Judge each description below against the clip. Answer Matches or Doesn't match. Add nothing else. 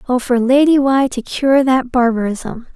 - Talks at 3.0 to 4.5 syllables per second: Matches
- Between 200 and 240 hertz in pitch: Doesn't match